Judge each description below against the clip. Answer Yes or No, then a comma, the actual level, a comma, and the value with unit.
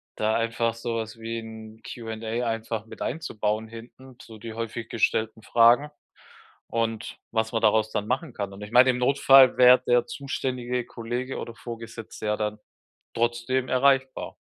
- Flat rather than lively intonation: Yes, narrow, 1.9 semitones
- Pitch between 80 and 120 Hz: Yes, low, 115 Hz